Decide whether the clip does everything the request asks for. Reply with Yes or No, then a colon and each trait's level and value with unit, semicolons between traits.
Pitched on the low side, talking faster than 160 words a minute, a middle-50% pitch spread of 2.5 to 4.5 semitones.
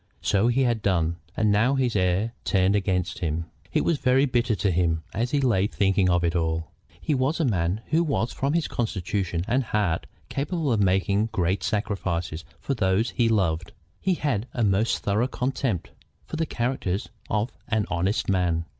No: low, 105 Hz; average, 180 wpm; average, 5.3 semitones